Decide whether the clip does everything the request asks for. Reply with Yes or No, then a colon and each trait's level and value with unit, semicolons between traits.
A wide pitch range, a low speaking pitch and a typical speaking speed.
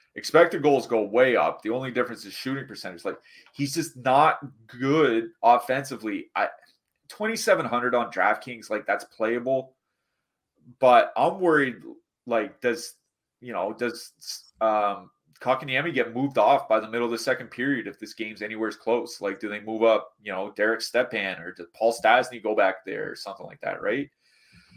Yes: wide, 6.6 semitones; low, 125 Hz; average, 170 wpm